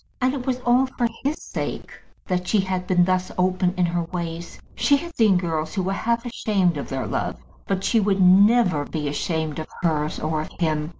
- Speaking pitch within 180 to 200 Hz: Yes, medium, 185 Hz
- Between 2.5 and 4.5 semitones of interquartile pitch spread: No, average, 5.0 semitones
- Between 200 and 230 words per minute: Yes, fast, 205 wpm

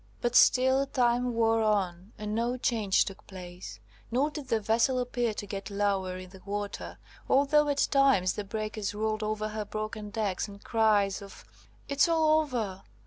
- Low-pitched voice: No, high, 215 Hz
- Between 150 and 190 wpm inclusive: Yes, average, 170 wpm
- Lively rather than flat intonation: No, average, 3.7 semitones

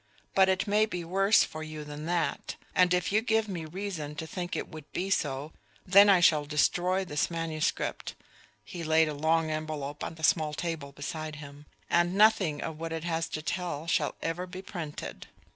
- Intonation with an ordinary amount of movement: Yes, average, 3.0 semitones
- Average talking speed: Yes, average, 195 wpm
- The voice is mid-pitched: Yes, medium, 165 Hz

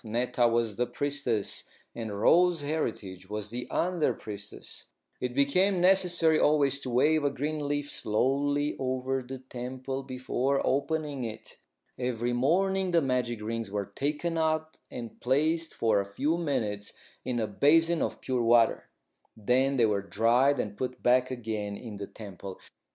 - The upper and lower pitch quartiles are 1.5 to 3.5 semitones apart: No, average, 4.4 semitones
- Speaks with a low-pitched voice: Yes, low, 130 Hz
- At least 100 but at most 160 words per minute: Yes, average, 150 wpm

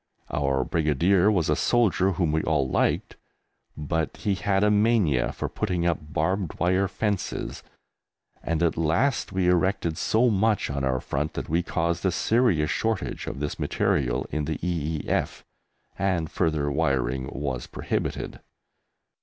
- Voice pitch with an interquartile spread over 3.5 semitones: Yes, average, 4.6 semitones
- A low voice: Yes, very low, 85 Hz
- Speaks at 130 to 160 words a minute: Yes, average, 145 wpm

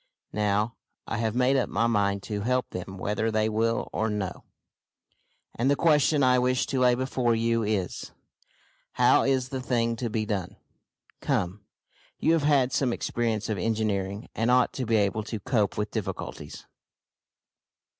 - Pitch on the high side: No, low, 115 Hz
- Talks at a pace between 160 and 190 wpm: Yes, average, 165 wpm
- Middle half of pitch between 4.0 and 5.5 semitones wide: No, average, 3.3 semitones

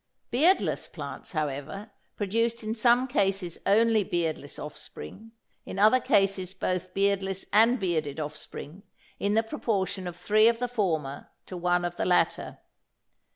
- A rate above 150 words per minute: No, average, 140 wpm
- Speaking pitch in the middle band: No, high, 195 Hz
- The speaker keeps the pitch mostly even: No, average, 4.2 semitones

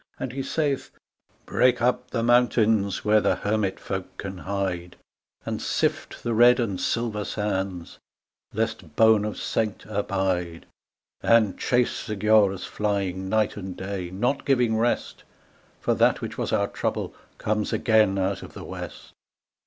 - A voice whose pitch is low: Yes, low, 105 Hz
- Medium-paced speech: Yes, average, 150 wpm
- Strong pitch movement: No, average, 3.3 semitones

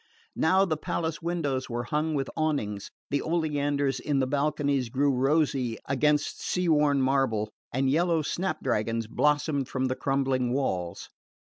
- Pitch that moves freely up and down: No, average, 2.8 semitones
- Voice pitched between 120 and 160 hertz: Yes, medium, 140 Hz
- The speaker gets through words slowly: No, average, 150 wpm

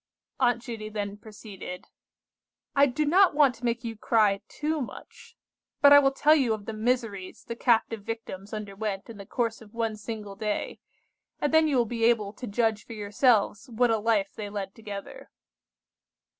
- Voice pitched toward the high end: Yes, high, 225 Hz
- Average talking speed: Yes, average, 180 wpm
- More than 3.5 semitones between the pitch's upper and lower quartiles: No, average, 3.0 semitones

